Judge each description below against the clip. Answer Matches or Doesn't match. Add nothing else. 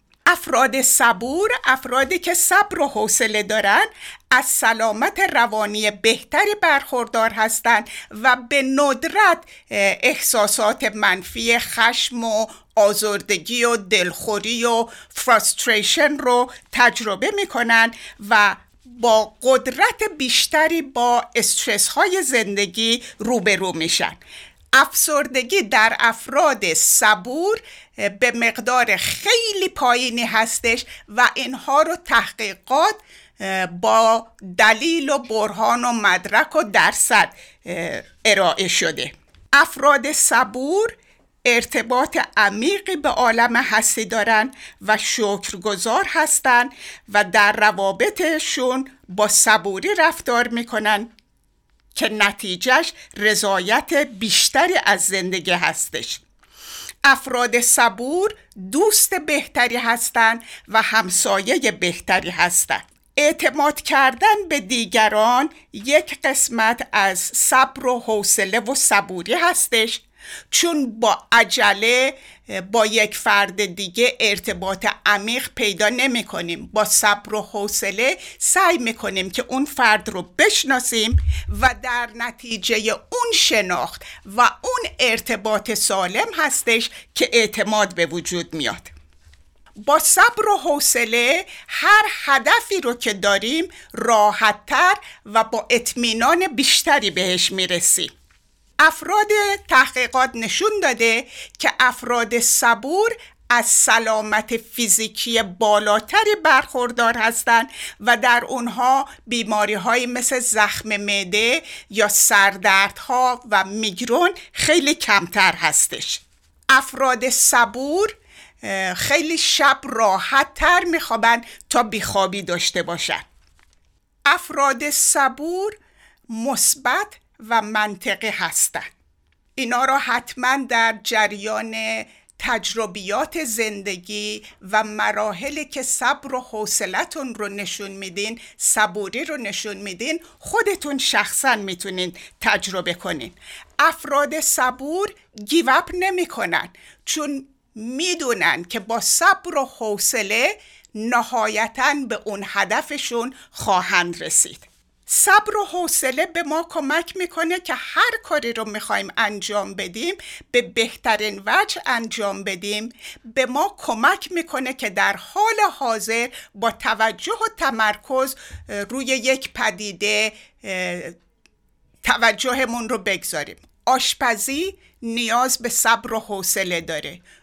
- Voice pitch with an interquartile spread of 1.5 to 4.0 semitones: Doesn't match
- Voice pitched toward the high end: Matches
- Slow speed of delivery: Matches